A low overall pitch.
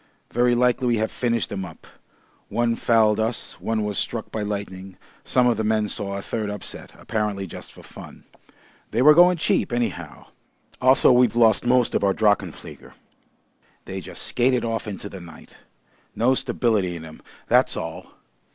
Yes: low, 110 Hz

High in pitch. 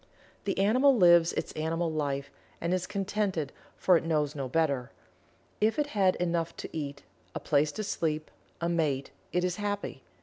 No: medium, 170 Hz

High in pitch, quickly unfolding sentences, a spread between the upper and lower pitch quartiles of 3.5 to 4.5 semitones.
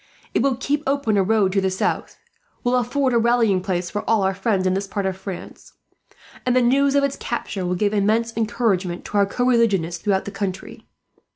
Yes: high, 210 Hz; fast, 210 wpm; average, 4.1 semitones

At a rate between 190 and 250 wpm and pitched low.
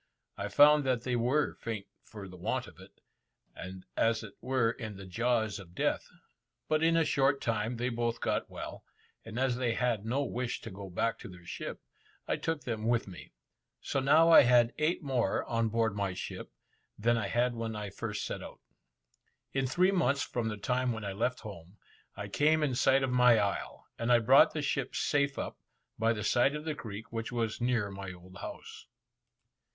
Yes: average, 200 wpm; low, 115 Hz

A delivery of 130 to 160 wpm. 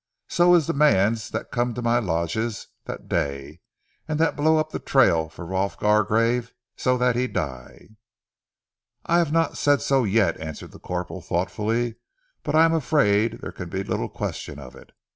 No: average, 185 wpm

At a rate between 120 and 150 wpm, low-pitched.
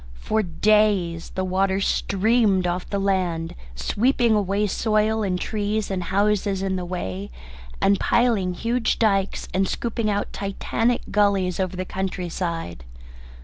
No: average, 140 wpm; high, 195 Hz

